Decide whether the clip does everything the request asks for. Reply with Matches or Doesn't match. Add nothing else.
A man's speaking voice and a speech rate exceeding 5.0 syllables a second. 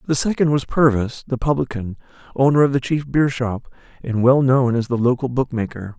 Matches